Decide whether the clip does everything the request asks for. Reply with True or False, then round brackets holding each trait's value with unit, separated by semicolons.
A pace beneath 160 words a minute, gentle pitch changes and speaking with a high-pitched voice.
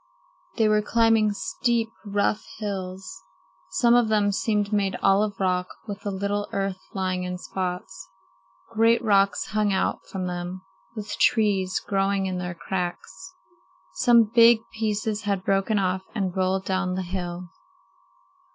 True (140 wpm; 2.3 semitones; 195 Hz)